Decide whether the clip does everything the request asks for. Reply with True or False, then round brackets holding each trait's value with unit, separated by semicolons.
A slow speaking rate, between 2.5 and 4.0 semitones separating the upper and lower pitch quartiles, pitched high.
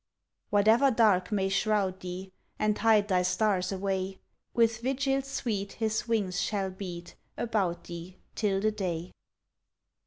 True (130 wpm; 2.9 semitones; 200 Hz)